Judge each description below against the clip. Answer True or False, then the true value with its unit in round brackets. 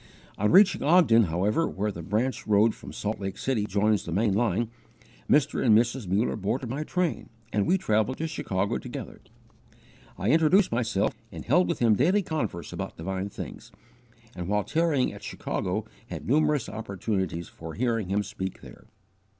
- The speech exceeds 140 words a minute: True (165 wpm)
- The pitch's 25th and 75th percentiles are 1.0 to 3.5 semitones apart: False (5.3 semitones)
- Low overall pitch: True (110 Hz)